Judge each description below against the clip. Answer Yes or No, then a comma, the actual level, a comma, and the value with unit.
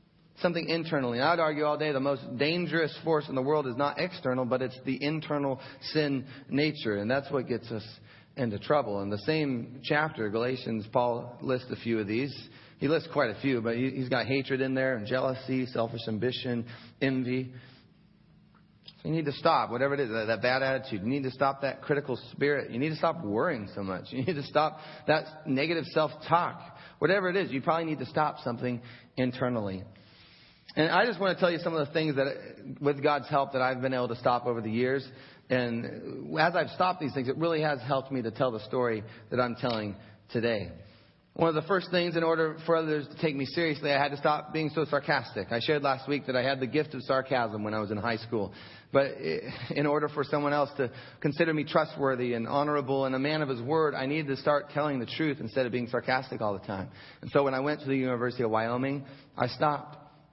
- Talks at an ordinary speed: No, fast, 225 wpm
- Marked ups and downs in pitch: No, average, 3.7 semitones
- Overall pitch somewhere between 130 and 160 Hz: Yes, low, 135 Hz